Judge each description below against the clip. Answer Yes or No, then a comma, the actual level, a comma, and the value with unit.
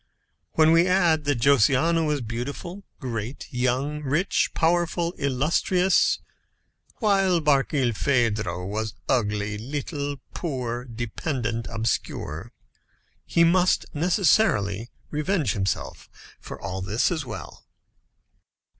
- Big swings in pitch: Yes, wide, 6.4 semitones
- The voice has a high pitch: No, medium, 140 Hz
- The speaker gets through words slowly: Yes, slow, 100 wpm